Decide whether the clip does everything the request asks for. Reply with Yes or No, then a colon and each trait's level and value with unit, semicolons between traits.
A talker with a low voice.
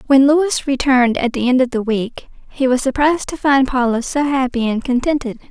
No: very high, 260 Hz